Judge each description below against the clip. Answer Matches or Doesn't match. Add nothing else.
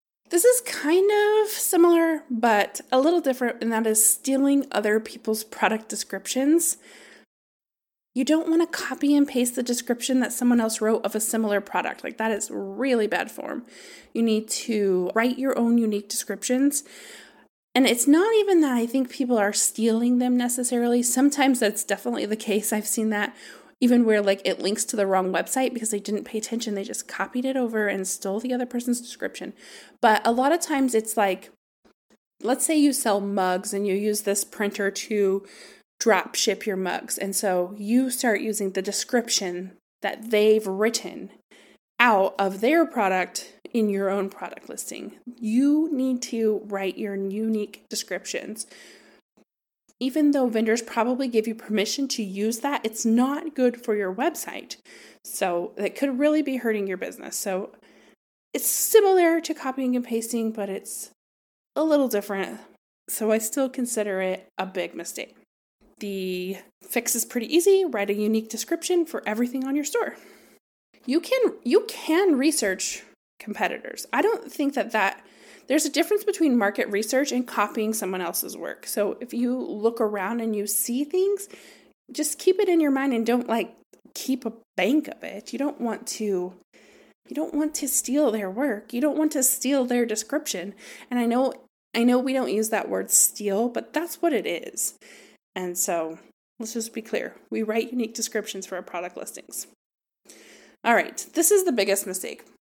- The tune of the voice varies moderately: Matches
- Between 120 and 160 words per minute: Doesn't match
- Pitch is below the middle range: Doesn't match